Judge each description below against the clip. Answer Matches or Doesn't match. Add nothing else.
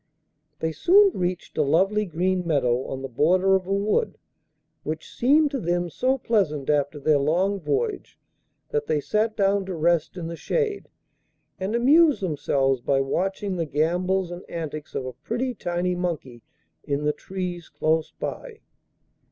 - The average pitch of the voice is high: Doesn't match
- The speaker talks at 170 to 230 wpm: Doesn't match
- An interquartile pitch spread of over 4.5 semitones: Matches